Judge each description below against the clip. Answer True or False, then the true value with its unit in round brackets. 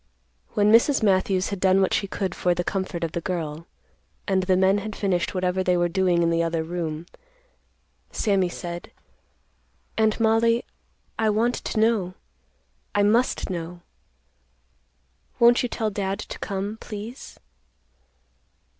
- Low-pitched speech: False (190 Hz)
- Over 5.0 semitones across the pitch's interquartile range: False (3.3 semitones)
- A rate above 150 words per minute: False (145 wpm)